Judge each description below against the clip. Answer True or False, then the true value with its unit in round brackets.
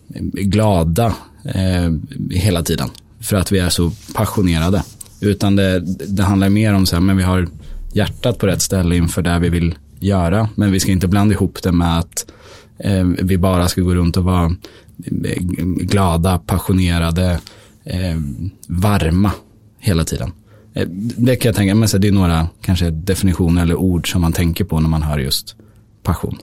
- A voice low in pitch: True (95 Hz)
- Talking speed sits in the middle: True (165 wpm)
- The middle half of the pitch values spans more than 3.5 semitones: False (2.7 semitones)